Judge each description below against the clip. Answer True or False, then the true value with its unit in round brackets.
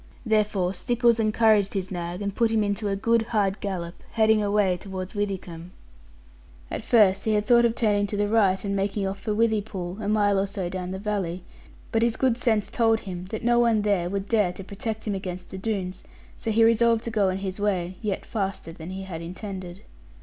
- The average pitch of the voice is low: False (205 Hz)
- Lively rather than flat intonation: False (2.7 semitones)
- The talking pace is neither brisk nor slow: False (210 wpm)